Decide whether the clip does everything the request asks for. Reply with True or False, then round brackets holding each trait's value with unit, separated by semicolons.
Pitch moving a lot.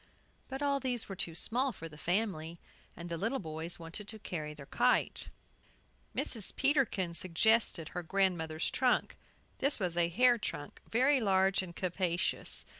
True (6.1 semitones)